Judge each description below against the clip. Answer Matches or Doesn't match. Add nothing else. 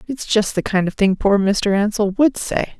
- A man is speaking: Doesn't match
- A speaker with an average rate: Doesn't match